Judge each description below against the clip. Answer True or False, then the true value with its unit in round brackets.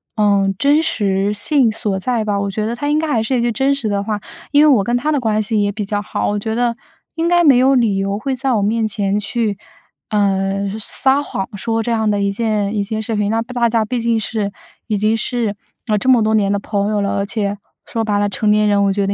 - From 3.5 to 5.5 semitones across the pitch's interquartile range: False (2.8 semitones)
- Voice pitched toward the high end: True (215 Hz)